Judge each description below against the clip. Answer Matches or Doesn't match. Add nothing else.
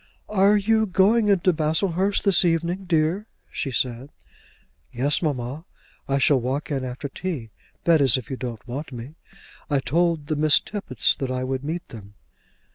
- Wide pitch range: Matches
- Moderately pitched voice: Matches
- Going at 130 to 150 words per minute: Doesn't match